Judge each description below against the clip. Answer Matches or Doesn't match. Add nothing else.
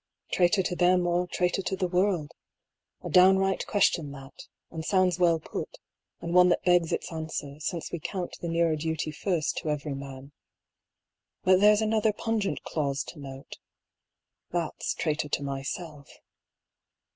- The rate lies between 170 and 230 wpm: Doesn't match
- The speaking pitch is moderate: Matches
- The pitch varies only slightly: Doesn't match